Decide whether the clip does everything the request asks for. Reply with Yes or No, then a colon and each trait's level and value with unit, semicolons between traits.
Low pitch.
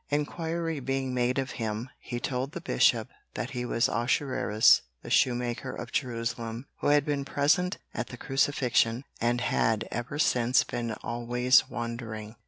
Yes: low, 125 Hz